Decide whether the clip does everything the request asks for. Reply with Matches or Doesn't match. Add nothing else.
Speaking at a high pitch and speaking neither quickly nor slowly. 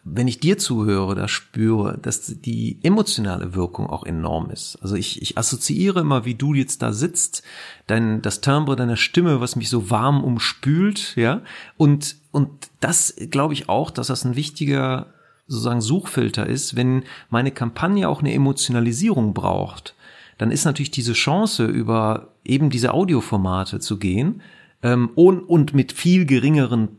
Doesn't match